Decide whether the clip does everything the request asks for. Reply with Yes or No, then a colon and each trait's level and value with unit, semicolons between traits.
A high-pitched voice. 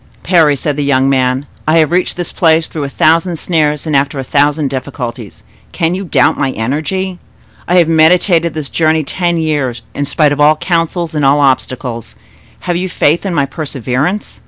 No: medium, 150 Hz